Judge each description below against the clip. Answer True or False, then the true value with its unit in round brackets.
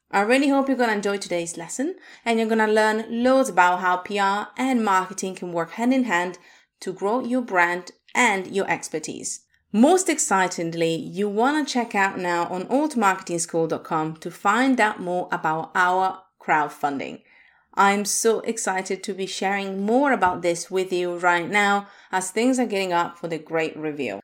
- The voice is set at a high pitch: True (195 Hz)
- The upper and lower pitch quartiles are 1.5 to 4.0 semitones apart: False (4.6 semitones)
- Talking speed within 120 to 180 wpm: True (175 wpm)